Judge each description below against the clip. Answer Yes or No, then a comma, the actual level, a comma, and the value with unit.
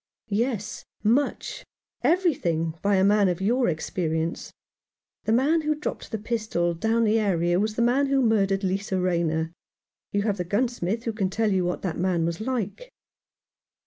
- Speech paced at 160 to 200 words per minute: Yes, average, 175 wpm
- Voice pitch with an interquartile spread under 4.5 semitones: No, average, 4.8 semitones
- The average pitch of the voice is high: Yes, high, 205 Hz